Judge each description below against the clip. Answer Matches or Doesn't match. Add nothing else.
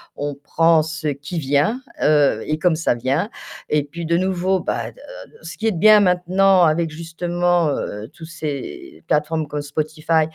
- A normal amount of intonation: Matches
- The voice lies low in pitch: Doesn't match